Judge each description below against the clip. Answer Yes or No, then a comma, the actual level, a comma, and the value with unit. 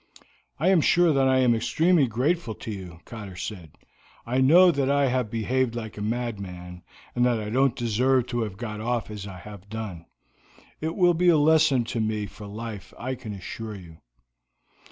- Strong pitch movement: No, average, 4.2 semitones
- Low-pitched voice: Yes, low, 115 Hz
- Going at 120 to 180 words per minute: No, average, 190 wpm